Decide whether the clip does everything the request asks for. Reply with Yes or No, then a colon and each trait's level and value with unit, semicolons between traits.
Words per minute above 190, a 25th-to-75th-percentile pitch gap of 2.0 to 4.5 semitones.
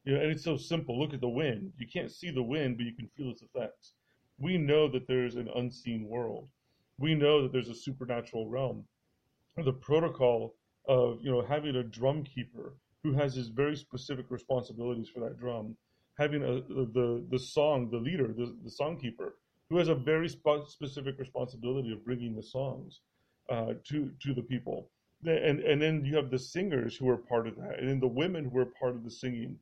Yes: fast, 205 wpm; average, 3.3 semitones